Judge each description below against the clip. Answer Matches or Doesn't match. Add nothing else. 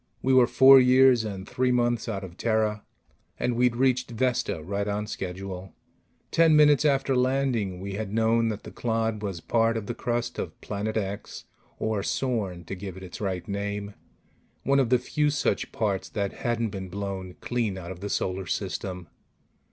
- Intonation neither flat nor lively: Matches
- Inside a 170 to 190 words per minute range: Matches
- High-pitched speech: Doesn't match